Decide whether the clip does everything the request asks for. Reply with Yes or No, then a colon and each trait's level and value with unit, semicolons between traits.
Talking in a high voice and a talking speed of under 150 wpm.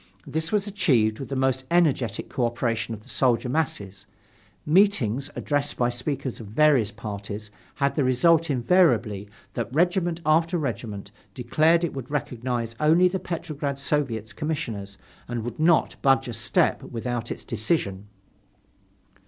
No: low, 130 Hz; average, 140 wpm